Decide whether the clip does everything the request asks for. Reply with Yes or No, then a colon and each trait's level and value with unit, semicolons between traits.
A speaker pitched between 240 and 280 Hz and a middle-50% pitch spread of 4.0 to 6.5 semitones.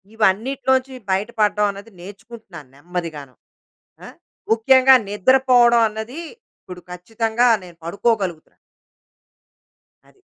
No: high, 215 Hz; average, 4.9 semitones